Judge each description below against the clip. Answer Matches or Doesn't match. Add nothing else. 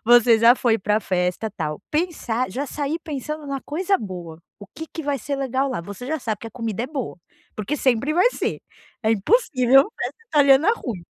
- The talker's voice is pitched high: Matches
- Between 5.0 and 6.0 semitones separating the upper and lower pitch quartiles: Matches